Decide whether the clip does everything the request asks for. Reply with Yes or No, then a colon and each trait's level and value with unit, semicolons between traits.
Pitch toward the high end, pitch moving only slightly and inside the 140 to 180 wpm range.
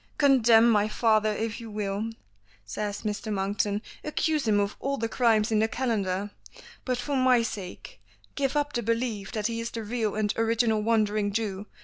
Yes: high, 220 Hz; narrow, 2.3 semitones; average, 175 wpm